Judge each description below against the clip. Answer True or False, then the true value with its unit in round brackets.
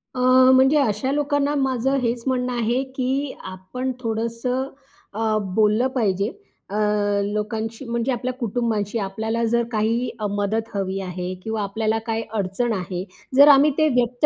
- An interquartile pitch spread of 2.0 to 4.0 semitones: True (3.2 semitones)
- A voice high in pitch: True (230 Hz)